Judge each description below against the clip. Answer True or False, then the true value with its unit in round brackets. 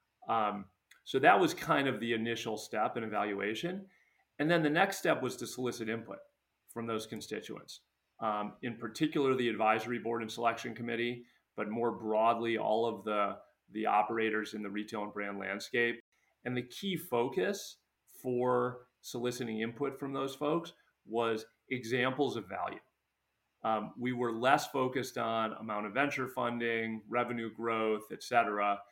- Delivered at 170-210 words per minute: False (155 wpm)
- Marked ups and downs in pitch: False (2.5 semitones)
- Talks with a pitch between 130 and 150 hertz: False (115 Hz)